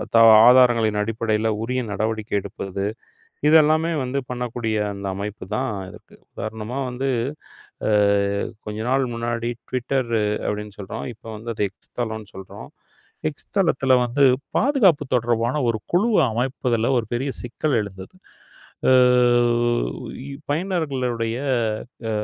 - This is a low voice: Yes, low, 120 Hz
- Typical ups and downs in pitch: Yes, average, 3.4 semitones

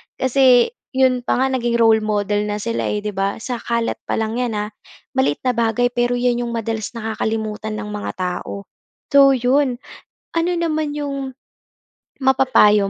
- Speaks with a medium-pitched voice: No, high, 235 Hz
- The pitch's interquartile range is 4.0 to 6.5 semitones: No, average, 3.4 semitones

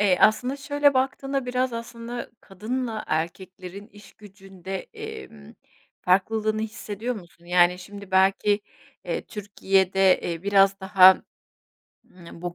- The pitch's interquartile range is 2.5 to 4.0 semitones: Yes, average, 3.6 semitones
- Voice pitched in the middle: No, high, 205 Hz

